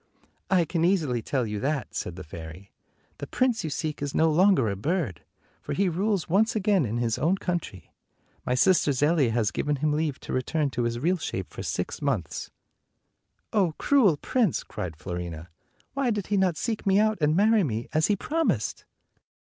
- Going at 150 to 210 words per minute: Yes, average, 190 wpm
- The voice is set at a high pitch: No, medium, 155 Hz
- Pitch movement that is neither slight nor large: No, wide, 8.4 semitones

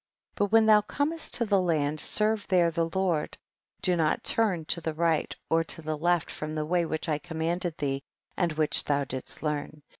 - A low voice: No, medium, 165 Hz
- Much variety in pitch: No, average, 3.2 semitones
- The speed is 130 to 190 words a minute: No, fast, 205 wpm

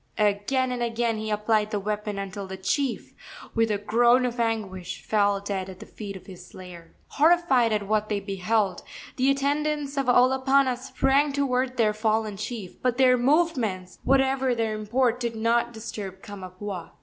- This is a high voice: Yes, high, 225 Hz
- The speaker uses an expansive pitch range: No, average, 4.1 semitones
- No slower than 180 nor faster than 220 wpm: No, average, 165 wpm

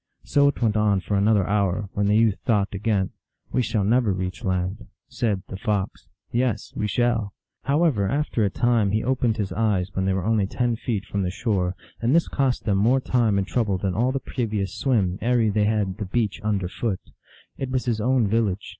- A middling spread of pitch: Yes, average, 3.5 semitones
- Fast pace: Yes, fast, 215 wpm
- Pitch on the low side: Yes, low, 105 Hz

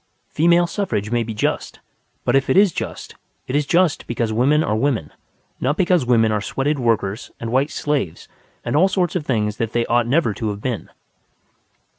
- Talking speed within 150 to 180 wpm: No, average, 190 wpm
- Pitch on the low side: Yes, low, 125 Hz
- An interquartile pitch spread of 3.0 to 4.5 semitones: No, average, 5.3 semitones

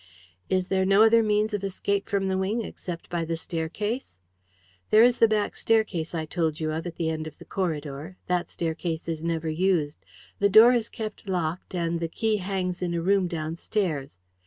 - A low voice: No, medium, 180 Hz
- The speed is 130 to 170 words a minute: No, average, 195 wpm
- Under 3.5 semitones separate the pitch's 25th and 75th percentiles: No, average, 3.8 semitones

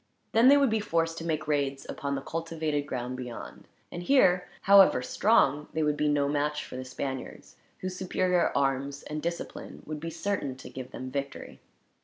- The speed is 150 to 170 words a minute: No, average, 185 wpm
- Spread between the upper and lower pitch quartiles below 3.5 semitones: No, average, 4.0 semitones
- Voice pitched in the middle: Yes, medium, 150 Hz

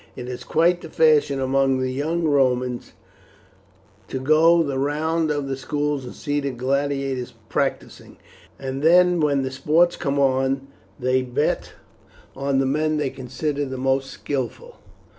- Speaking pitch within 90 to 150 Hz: Yes, medium, 140 Hz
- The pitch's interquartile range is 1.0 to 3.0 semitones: Yes, narrow, 2.6 semitones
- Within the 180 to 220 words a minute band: No, average, 150 wpm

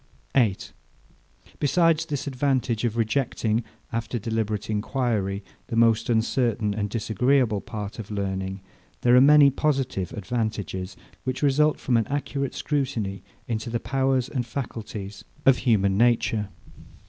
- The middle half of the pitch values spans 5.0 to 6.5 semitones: No, average, 4.1 semitones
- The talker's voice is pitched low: Yes, low, 115 Hz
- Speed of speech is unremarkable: No, slow, 125 wpm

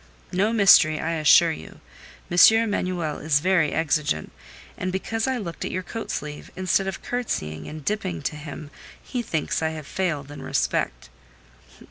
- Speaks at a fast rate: No, average, 160 wpm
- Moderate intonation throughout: Yes, average, 4.2 semitones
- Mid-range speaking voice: Yes, medium, 165 Hz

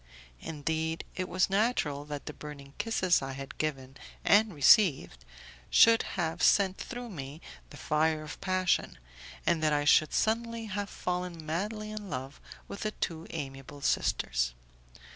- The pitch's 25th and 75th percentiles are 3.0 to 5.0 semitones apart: No, wide, 5.5 semitones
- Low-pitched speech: No, medium, 160 Hz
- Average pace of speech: Yes, average, 145 wpm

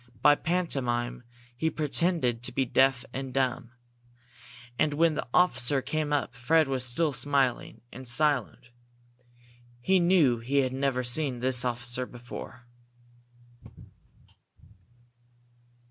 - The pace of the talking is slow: Yes, slow, 115 wpm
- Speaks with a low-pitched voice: Yes, low, 130 Hz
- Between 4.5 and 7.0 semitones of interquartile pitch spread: No, average, 3.4 semitones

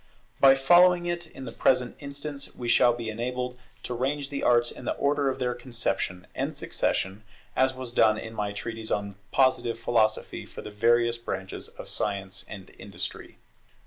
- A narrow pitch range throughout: No, average, 3.6 semitones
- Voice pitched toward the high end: No, low, 120 Hz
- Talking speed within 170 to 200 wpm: Yes, average, 175 wpm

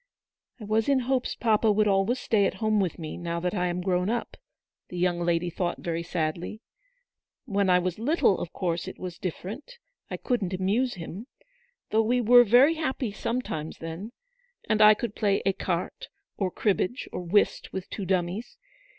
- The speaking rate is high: No, average, 190 wpm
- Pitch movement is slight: No, average, 4.3 semitones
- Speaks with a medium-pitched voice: No, high, 195 Hz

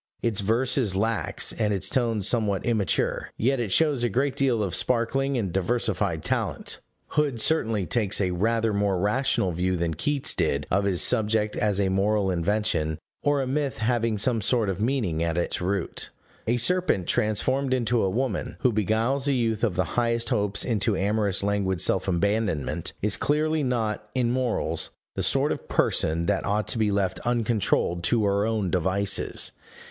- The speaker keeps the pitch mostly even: No, average, 3.9 semitones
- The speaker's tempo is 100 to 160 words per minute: No, average, 175 wpm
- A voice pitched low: Yes, low, 110 Hz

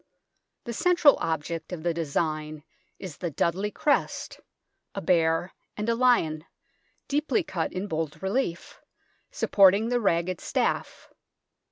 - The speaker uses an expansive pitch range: Yes, wide, 6.0 semitones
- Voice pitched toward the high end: No, medium, 180 Hz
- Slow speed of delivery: Yes, slow, 125 wpm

